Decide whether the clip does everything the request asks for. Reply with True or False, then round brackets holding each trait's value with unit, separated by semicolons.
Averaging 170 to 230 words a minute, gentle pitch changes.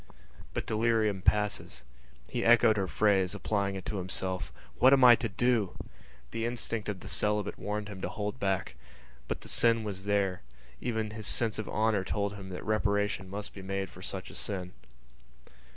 True (180 wpm; 2.2 semitones)